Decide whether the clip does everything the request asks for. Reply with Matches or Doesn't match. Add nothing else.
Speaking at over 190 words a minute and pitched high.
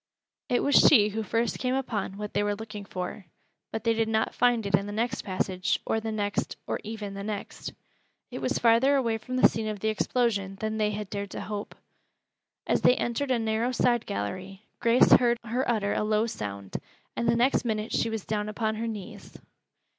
Matches